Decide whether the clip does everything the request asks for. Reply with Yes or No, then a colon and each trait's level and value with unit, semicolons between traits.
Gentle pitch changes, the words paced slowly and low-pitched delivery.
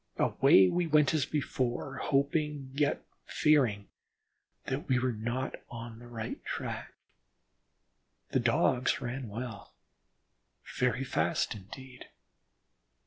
No: average, 3.3 semitones; slow, 105 wpm; low, 125 Hz